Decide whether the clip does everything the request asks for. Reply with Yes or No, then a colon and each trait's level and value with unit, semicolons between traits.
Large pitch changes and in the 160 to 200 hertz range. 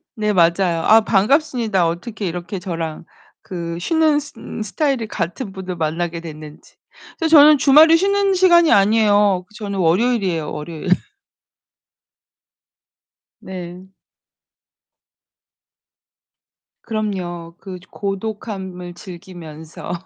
No: average, 4.8 semitones; high, 190 Hz